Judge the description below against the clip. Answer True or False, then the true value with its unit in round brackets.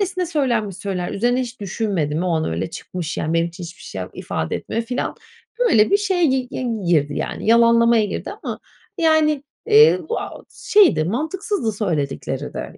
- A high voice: True (230 Hz)